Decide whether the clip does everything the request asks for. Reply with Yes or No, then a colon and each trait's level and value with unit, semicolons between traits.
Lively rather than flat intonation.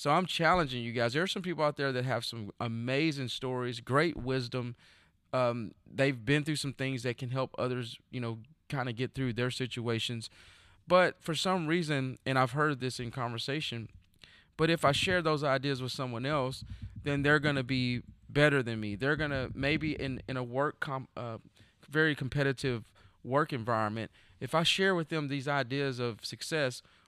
No: average, 3.7 semitones